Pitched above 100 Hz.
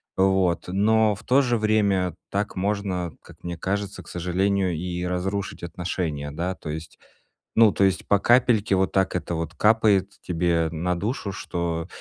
No: very low, 95 Hz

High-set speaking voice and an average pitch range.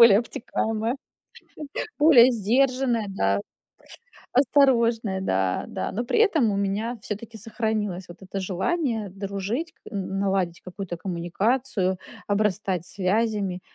Yes: high, 210 Hz; average, 3.7 semitones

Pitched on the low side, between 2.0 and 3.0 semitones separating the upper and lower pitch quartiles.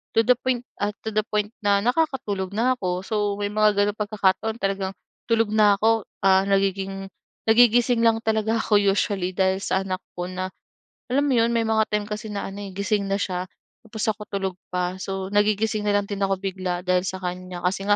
No: high, 205 Hz; narrow, 2.4 semitones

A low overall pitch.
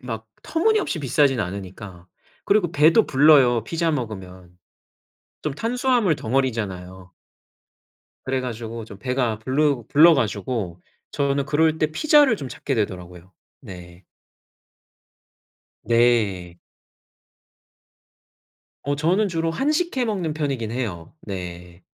Yes: low, 125 Hz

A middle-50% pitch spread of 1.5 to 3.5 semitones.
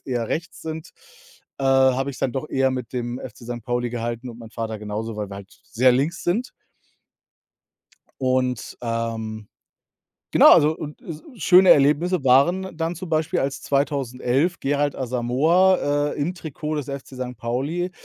No: average, 4.3 semitones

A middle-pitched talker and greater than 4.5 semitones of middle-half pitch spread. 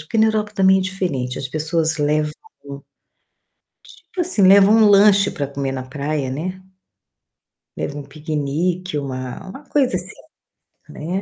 Yes: medium, 165 Hz; average, 5.2 semitones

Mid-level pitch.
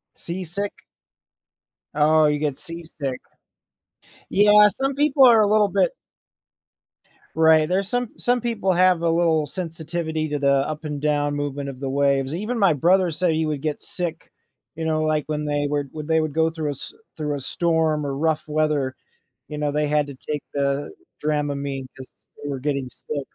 Yes: medium, 155 Hz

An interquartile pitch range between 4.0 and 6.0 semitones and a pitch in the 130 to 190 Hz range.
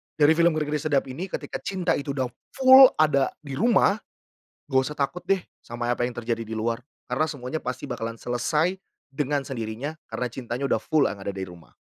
Yes: average, 4.5 semitones; medium, 140 Hz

